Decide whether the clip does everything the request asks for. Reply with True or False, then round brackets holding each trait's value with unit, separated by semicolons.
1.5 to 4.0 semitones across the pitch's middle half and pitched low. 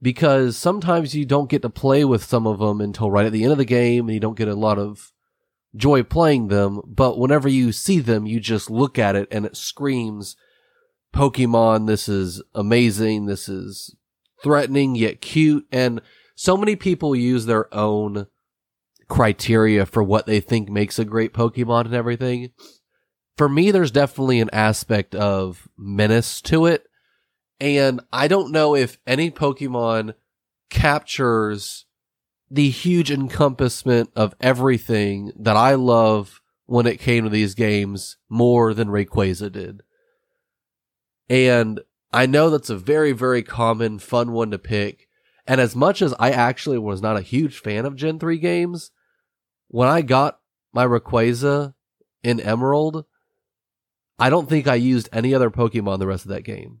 False (4.6 semitones; 120 Hz)